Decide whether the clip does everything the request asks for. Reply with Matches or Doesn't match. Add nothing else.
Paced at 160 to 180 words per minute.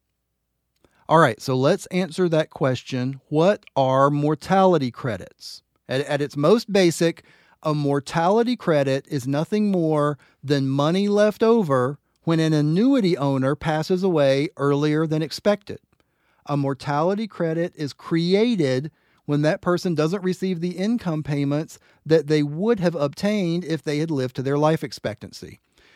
Doesn't match